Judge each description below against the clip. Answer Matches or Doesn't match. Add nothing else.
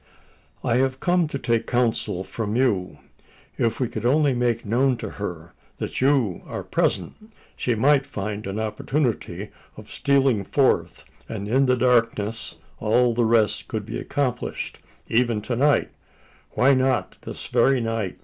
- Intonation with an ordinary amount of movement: Matches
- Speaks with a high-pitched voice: Doesn't match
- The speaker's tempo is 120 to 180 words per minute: Matches